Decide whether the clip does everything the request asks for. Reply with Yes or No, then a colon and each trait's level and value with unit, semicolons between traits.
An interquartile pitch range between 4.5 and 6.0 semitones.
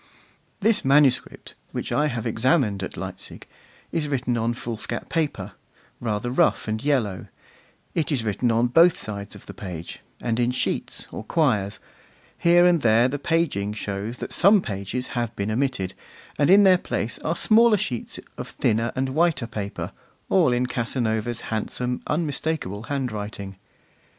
Yes: wide, 5.5 semitones